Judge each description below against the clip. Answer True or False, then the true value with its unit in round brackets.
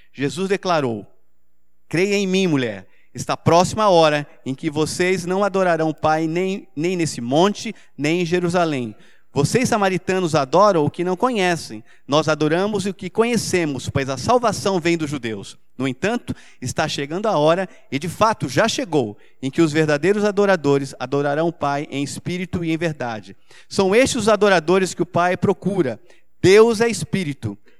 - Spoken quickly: False (165 wpm)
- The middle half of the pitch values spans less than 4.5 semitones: False (5.1 semitones)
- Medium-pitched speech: True (170 Hz)